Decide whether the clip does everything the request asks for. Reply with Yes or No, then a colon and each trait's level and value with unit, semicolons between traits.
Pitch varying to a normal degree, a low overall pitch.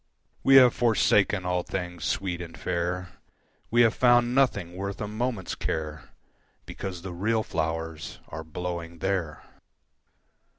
Yes: average, 4.6 semitones; very low, 90 Hz